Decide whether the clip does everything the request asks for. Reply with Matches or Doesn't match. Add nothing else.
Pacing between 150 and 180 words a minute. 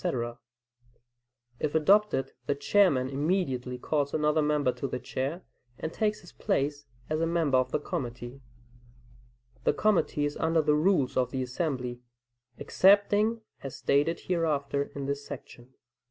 Doesn't match